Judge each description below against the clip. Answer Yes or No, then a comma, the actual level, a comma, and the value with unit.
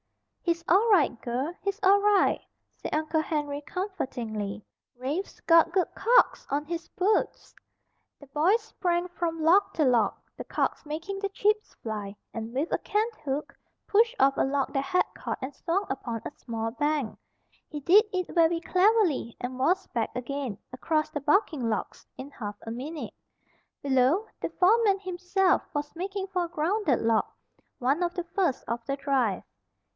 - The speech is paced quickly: No, average, 165 wpm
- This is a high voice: Yes, very high, 315 Hz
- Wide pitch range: Yes, wide, 6.2 semitones